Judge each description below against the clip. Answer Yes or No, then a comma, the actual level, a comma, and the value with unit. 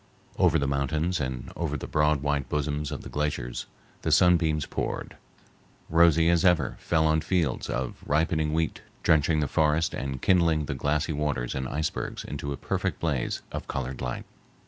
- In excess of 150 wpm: Yes, average, 170 wpm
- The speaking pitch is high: No, very low, 75 Hz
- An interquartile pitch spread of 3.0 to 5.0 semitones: No, narrow, 2.6 semitones